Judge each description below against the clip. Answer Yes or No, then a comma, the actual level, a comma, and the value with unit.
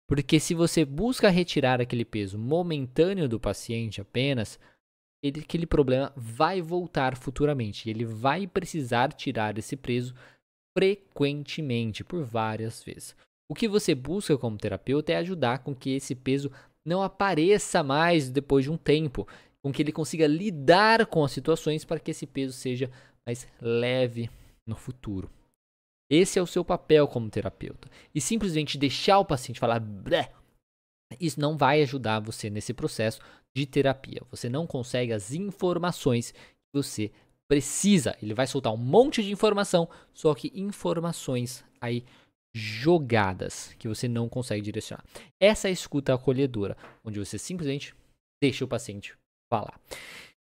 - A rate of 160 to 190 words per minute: No, average, 145 wpm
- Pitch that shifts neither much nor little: No, wide, 5.7 semitones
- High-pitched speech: No, medium, 140 Hz